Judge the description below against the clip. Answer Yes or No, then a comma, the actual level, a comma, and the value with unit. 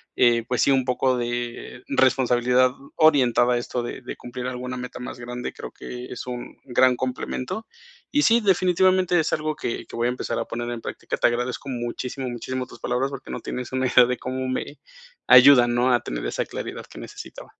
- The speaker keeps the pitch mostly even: Yes, narrow, 1.3 semitones